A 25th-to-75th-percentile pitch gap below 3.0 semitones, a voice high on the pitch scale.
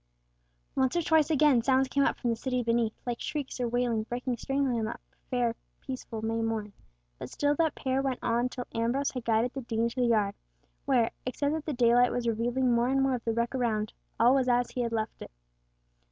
Yes: narrow, 2.4 semitones; high, 245 Hz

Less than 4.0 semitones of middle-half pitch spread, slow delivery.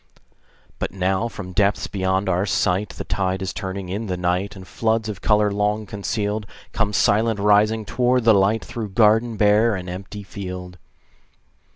No: narrow, 2.4 semitones; average, 165 wpm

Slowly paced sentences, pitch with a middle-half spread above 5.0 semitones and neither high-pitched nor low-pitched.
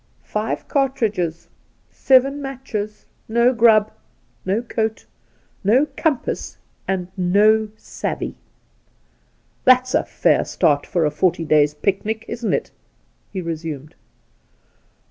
No: slow, 105 wpm; wide, 5.4 semitones; high, 215 Hz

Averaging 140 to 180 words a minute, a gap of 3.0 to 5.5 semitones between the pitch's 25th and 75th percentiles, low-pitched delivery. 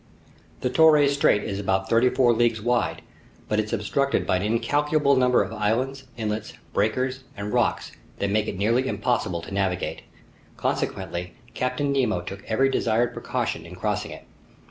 Yes: average, 160 wpm; average, 4.2 semitones; low, 115 Hz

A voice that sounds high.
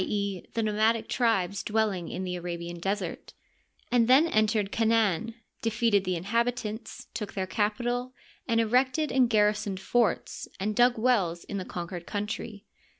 Yes: high, 215 Hz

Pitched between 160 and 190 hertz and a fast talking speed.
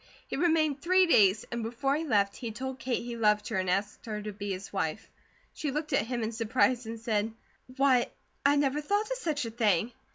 No: high, 235 Hz; fast, 220 wpm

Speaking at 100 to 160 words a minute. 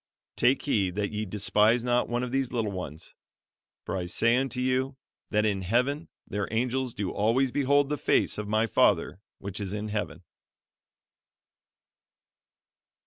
Yes: average, 150 wpm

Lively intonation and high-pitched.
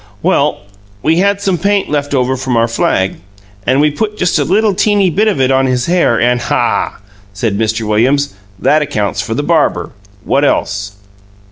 No: wide, 7.7 semitones; medium, 140 Hz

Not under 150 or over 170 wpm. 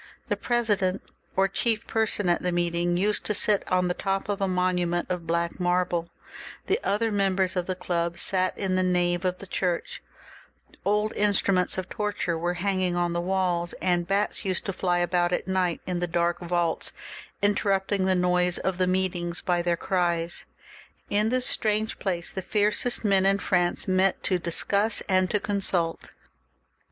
No: average, 180 wpm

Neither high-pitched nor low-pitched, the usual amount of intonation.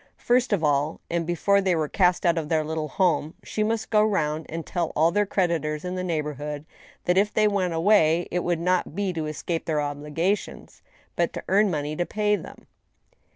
Yes: medium, 170 Hz; average, 4.3 semitones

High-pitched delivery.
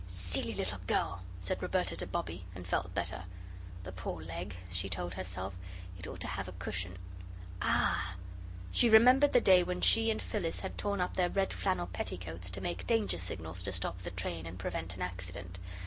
No: very low, 90 Hz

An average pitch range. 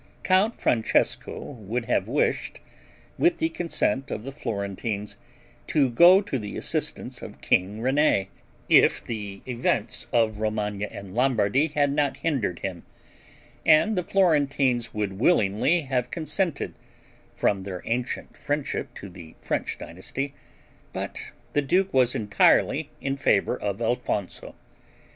No: wide, 6.0 semitones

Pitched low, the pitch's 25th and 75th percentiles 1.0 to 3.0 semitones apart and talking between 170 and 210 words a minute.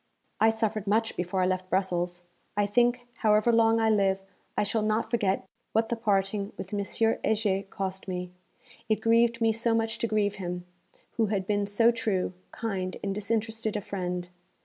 No: high, 210 Hz; average, 2.7 semitones; average, 175 wpm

